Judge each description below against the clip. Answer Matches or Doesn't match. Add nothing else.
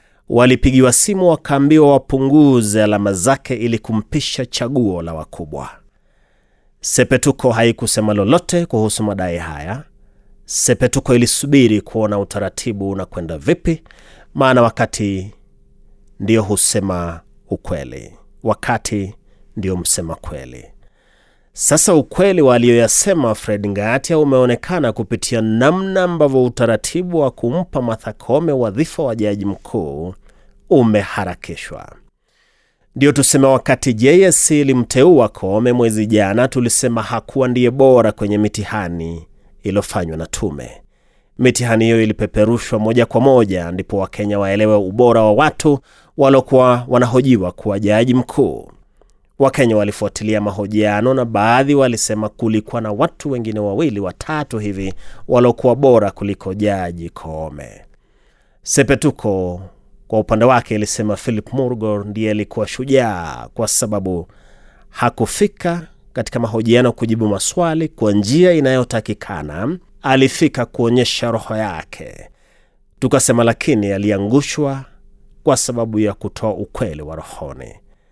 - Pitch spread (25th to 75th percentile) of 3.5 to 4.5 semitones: Matches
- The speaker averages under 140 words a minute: Matches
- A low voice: Matches